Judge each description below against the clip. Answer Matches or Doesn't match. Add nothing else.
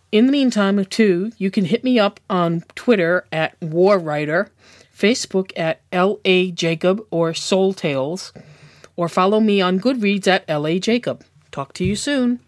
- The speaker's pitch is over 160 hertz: Matches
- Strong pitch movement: Doesn't match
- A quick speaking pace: Doesn't match